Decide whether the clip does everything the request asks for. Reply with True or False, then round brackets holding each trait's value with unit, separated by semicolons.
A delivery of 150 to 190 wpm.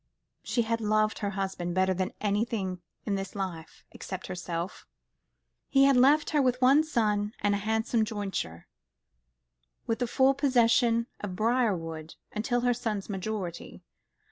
False (140 wpm)